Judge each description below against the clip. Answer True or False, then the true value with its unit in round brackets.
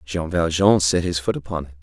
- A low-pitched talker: True (80 Hz)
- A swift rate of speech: True (230 wpm)